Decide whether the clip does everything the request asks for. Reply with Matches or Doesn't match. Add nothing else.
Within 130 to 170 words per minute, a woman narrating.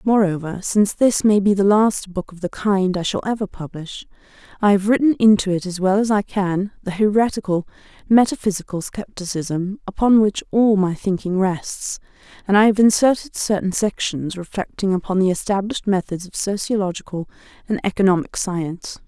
Matches